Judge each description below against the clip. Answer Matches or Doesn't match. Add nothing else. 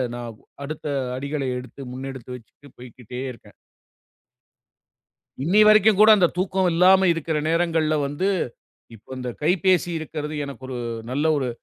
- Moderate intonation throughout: Doesn't match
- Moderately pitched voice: Matches